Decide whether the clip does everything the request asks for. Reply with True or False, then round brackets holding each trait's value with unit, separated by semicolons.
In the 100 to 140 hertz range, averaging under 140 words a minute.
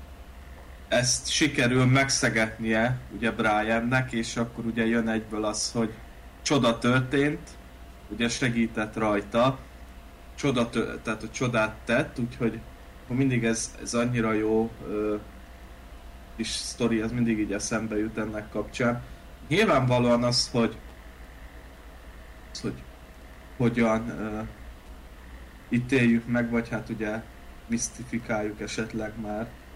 True (110 Hz; 105 wpm)